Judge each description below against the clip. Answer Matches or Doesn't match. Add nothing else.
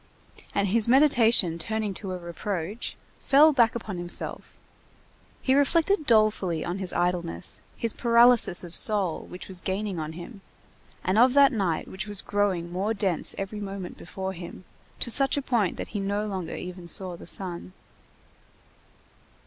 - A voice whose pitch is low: Doesn't match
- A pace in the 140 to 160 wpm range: Matches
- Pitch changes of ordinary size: Matches